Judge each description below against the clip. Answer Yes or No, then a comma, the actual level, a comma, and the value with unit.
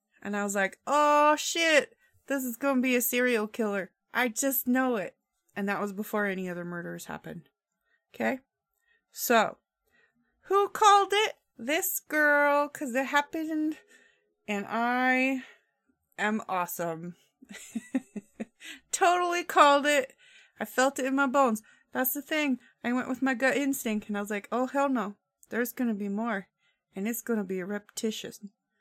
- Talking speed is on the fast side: No, average, 155 wpm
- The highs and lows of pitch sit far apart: Yes, wide, 5.8 semitones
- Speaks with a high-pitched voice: Yes, very high, 255 Hz